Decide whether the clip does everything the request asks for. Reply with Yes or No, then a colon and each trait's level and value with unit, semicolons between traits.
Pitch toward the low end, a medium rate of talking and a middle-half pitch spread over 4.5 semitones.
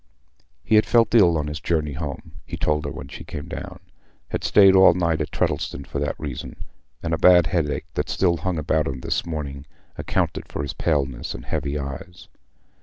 No: very low, 75 Hz; average, 185 wpm; average, 3.4 semitones